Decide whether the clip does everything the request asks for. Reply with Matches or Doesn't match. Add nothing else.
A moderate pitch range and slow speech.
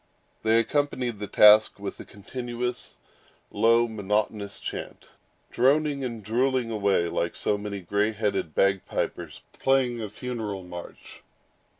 Matches